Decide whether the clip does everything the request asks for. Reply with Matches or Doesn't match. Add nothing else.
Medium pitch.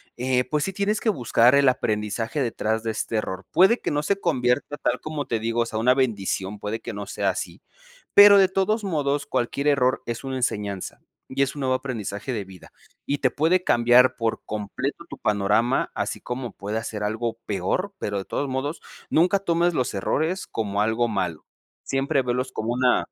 Doesn't match